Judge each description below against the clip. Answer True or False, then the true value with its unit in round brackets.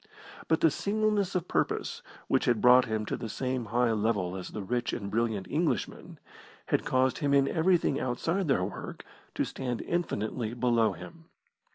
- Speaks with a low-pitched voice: True (125 Hz)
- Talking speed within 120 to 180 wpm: True (170 wpm)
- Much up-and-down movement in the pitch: True (6.5 semitones)